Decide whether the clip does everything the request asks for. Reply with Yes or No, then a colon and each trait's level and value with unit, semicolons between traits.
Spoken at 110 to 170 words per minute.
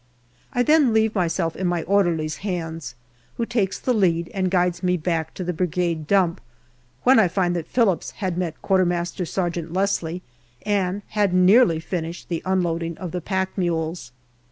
Yes: average, 160 wpm